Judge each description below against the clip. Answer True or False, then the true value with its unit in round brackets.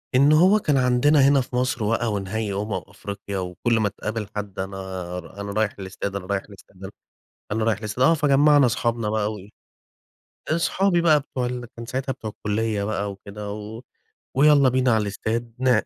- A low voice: True (110 Hz)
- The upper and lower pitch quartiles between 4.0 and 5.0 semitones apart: True (4.3 semitones)